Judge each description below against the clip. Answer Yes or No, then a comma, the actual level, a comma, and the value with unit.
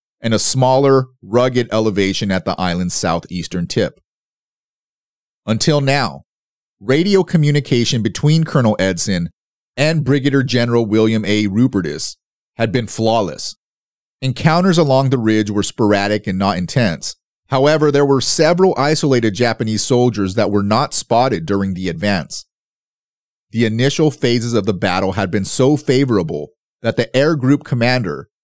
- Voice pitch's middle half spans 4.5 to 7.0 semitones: Yes, average, 4.9 semitones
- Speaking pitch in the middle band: No, low, 115 Hz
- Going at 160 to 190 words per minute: No, slow, 135 wpm